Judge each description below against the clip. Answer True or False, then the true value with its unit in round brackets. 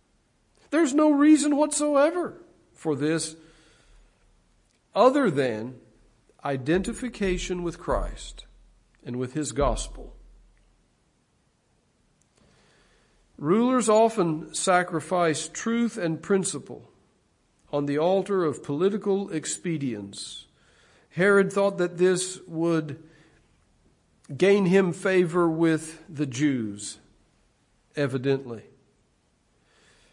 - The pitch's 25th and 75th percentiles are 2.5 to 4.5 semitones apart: False (5.2 semitones)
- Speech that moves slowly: True (80 wpm)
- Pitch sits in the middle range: True (165 Hz)